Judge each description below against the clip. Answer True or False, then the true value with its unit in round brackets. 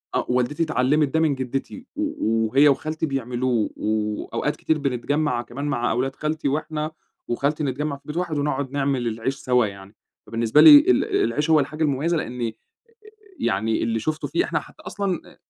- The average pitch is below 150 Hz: True (140 Hz)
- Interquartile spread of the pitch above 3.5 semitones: True (4.1 semitones)